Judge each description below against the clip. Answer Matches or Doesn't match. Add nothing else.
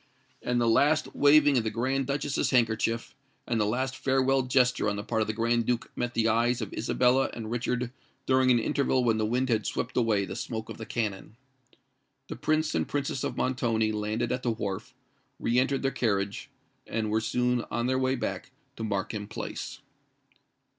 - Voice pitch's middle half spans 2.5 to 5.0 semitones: Matches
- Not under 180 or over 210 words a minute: Matches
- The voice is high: Doesn't match